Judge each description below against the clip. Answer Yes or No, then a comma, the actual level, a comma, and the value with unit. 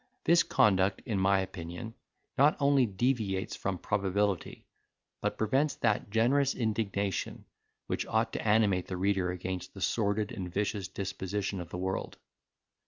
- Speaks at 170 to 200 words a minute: No, average, 140 wpm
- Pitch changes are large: No, average, 2.9 semitones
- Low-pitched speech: Yes, low, 100 Hz